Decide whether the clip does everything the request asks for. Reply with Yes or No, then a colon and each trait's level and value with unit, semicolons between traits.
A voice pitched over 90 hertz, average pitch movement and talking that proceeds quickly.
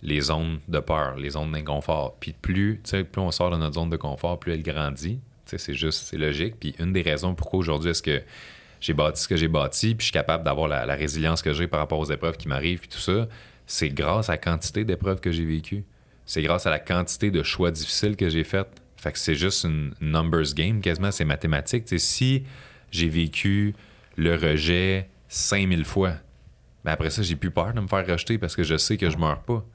No: very low, 85 Hz; average, 3.8 semitones; fast, 230 wpm